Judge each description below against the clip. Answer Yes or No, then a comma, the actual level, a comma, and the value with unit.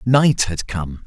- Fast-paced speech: No, average, 170 wpm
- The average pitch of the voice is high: No, low, 105 Hz